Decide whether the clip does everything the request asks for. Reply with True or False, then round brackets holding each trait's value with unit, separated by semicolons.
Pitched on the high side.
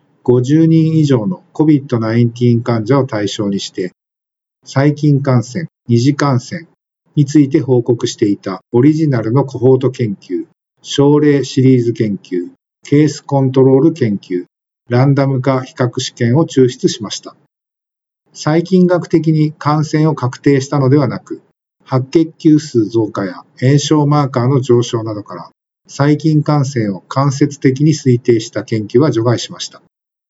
False (135 Hz)